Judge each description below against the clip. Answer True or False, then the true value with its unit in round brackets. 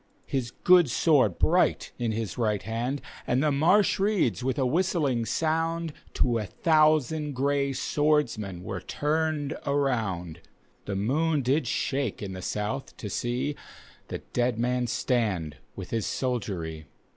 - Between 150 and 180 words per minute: False (140 wpm)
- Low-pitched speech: True (125 Hz)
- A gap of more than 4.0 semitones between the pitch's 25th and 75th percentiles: True (5.6 semitones)